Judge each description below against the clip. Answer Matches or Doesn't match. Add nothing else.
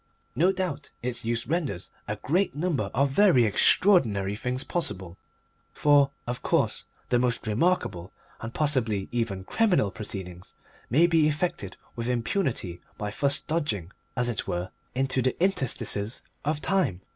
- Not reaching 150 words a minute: Matches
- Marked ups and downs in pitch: Matches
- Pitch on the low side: Matches